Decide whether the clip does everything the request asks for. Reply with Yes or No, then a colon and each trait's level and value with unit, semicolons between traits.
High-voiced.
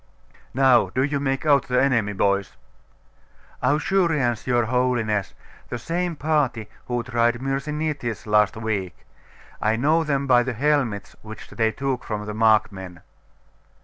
No: low, 120 Hz